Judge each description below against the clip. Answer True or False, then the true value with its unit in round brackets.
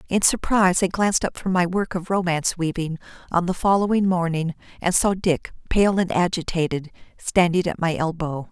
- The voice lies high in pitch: False (175 Hz)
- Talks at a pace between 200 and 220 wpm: False (175 wpm)